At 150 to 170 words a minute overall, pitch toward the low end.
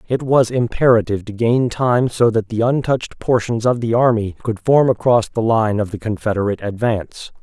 No: average, 185 wpm; low, 115 Hz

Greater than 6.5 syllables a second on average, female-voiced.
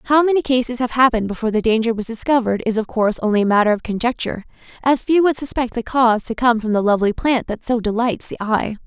Yes: 6.8 syllables/s; female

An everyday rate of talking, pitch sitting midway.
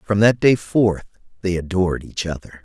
No: average, 180 wpm; very low, 95 Hz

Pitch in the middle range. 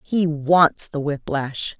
Yes: medium, 155 Hz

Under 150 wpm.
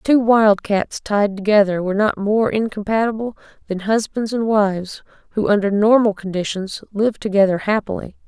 Yes: average, 140 wpm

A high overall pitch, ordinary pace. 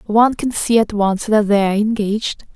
Yes: high, 215 Hz; average, 190 wpm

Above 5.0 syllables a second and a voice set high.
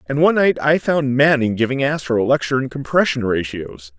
No: 5.8 syllables/s; low, 130 Hz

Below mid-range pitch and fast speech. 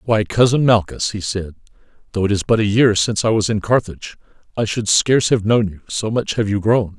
Yes: low, 105 Hz; fast, 230 wpm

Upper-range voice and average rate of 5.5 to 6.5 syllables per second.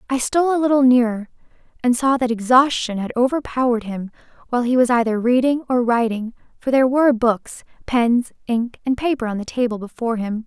Yes: high, 245 Hz; 5.9 syllables/s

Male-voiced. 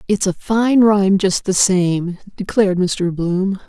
No: female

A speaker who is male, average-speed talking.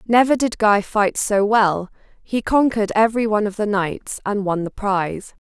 No: female; average, 185 wpm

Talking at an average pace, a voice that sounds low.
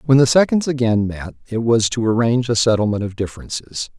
Yes: average, 195 wpm; low, 115 Hz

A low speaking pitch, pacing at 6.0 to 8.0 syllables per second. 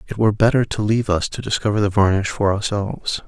Yes: low, 105 Hz; 6.5 syllables/s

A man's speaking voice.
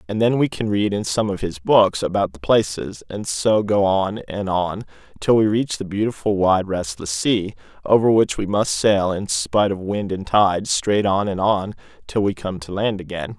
Yes: male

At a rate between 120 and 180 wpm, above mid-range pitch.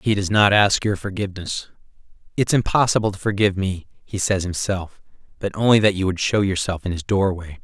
No: average, 175 wpm; very low, 95 Hz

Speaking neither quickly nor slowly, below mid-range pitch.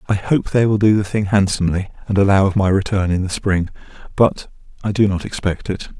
No: fast, 220 wpm; low, 100 Hz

